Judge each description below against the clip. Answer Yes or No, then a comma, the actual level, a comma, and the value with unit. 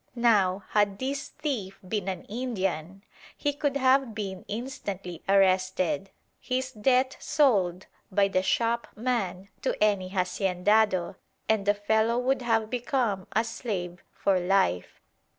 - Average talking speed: No, slow, 125 wpm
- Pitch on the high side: Yes, high, 205 Hz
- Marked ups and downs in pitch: No, average, 4.4 semitones